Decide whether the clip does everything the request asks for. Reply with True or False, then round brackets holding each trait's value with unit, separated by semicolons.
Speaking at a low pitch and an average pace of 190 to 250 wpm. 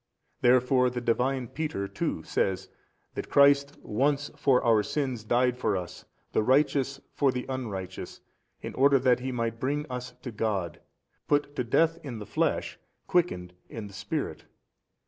False (125 Hz; 160 wpm)